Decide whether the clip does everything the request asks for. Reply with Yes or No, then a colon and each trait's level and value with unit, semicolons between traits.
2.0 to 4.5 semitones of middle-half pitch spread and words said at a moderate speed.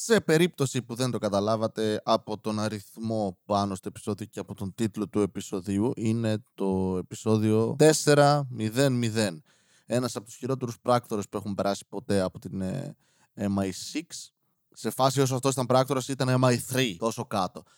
Yes: average, 4.1 semitones; average, 150 wpm